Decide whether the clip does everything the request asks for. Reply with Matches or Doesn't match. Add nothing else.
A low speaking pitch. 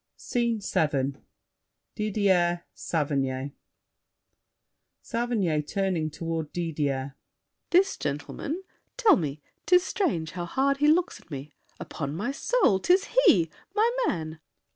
Doesn't match